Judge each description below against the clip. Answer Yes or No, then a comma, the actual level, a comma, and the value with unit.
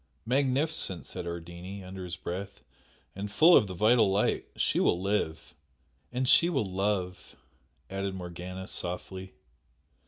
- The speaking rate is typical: No, slow, 130 wpm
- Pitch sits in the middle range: No, very low, 95 Hz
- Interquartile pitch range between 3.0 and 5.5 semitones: No, narrow, 2.6 semitones